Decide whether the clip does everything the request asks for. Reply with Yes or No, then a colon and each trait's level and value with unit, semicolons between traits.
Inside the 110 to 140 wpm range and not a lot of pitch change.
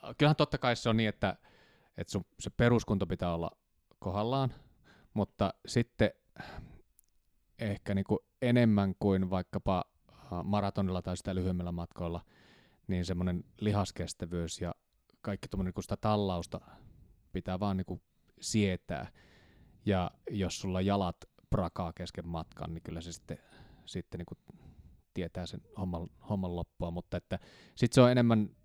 No: average, 130 wpm; average, 3.0 semitones